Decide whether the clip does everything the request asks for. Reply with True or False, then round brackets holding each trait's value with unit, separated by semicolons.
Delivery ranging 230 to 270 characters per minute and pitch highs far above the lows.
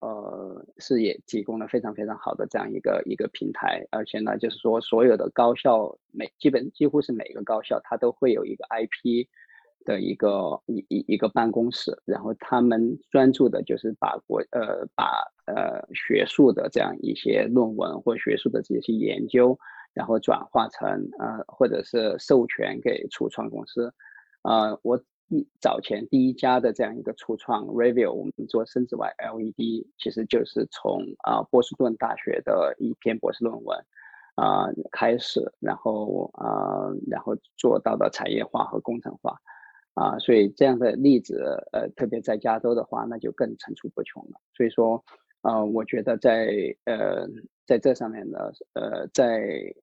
False (255 characters per minute; 2.9 semitones)